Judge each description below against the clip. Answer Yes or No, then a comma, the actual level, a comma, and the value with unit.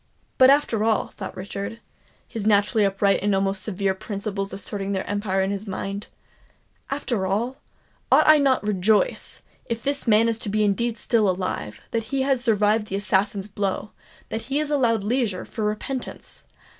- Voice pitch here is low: No, high, 210 Hz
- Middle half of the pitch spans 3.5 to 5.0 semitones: No, average, 2.8 semitones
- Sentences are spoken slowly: No, average, 155 wpm